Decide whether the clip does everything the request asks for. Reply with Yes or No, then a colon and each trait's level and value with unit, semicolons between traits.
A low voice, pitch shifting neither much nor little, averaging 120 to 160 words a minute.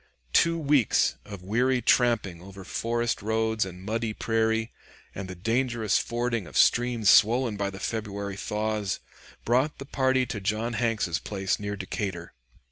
Yes: low, 110 Hz; average, 3.1 semitones; average, 145 wpm